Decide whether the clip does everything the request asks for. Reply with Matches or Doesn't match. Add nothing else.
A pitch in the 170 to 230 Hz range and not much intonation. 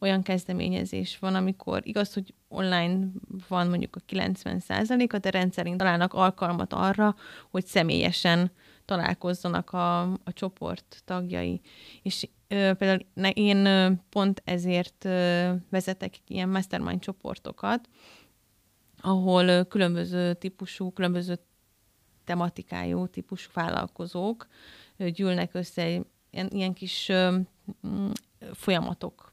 Matches